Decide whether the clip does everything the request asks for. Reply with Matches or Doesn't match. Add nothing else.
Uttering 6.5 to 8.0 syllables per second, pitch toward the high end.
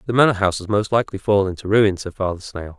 Doesn't match